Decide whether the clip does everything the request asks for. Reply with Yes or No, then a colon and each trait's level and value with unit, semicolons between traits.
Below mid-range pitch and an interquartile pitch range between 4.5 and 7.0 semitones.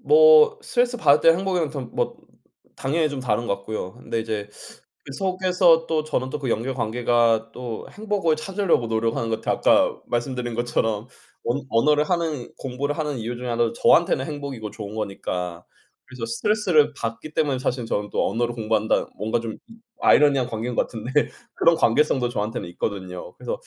Yes: low, 125 Hz; wide, 5.5 semitones